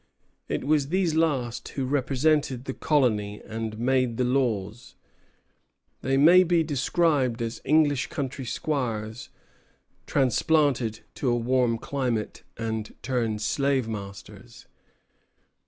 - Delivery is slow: Yes, slow, 110 wpm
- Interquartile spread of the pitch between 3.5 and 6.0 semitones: Yes, average, 4.1 semitones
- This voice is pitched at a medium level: No, low, 130 Hz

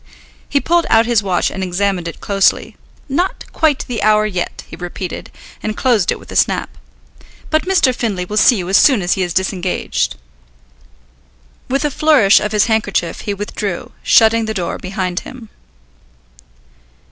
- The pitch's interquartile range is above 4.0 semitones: Yes, average, 4.6 semitones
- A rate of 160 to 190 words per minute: Yes, average, 165 wpm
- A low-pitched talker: No, high, 210 Hz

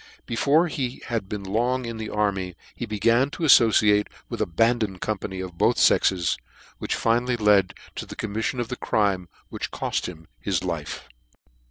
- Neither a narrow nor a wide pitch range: Yes, average, 3.9 semitones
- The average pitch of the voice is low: Yes, low, 105 Hz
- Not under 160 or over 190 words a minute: Yes, average, 165 wpm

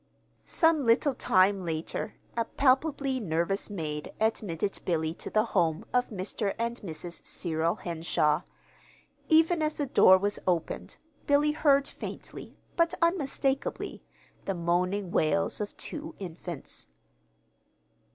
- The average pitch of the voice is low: No, high, 205 Hz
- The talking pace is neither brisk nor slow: No, slow, 120 wpm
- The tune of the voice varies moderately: No, wide, 8.2 semitones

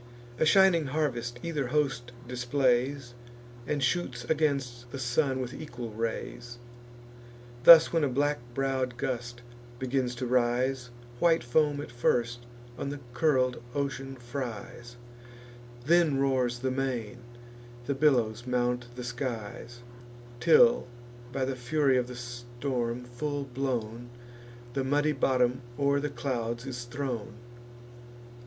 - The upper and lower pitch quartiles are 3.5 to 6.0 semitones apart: No, narrow, 2.6 semitones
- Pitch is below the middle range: Yes, low, 130 Hz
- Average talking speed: No, slow, 120 wpm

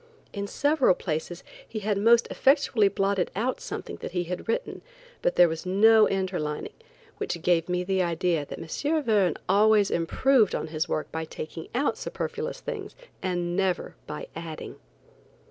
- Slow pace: No, average, 155 wpm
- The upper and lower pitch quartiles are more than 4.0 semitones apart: Yes, average, 4.4 semitones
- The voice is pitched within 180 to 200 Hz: Yes, high, 190 Hz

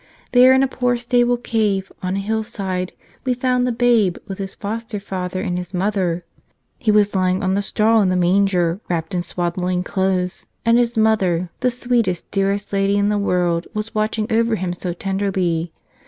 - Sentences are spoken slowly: No, average, 185 wpm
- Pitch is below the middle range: No, high, 195 Hz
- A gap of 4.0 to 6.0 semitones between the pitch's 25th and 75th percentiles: No, average, 3.6 semitones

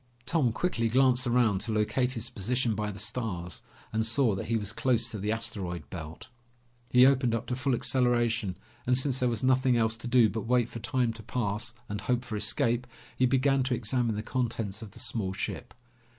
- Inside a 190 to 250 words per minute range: Yes, fast, 205 wpm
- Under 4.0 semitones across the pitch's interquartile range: Yes, average, 2.9 semitones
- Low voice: Yes, low, 115 Hz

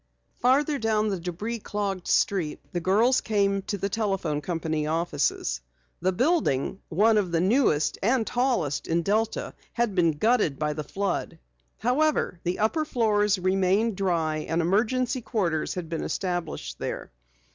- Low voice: No, high, 195 Hz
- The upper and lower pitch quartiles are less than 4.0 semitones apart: No, average, 5.0 semitones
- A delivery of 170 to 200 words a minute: No, average, 145 wpm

